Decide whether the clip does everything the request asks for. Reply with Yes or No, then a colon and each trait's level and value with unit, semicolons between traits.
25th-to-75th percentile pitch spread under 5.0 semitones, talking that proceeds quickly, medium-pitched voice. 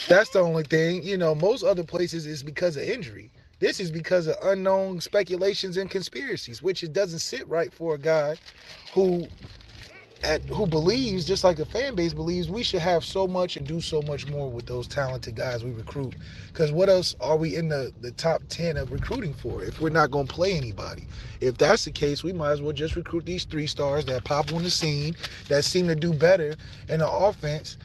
Yes: average, 4.0 semitones; fast, 215 wpm; medium, 155 Hz